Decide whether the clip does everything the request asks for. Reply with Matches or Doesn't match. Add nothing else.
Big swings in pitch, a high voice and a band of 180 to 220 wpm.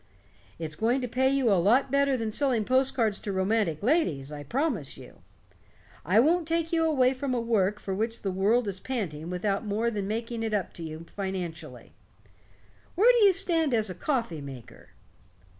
Matches